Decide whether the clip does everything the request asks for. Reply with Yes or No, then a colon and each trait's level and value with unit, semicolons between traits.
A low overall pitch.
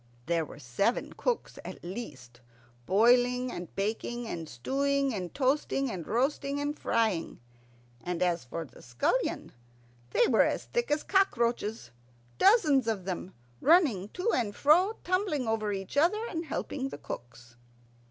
No: high, 235 Hz